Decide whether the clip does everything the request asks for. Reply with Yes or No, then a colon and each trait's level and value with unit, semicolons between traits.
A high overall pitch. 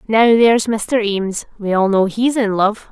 Yes: high, 210 Hz